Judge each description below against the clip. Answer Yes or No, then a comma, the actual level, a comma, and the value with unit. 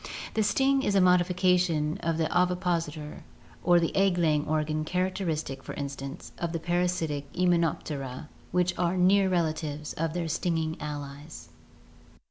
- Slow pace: Yes, slow, 130 wpm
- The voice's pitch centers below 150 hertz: No, medium, 170 Hz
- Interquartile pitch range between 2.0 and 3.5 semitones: Yes, average, 3.0 semitones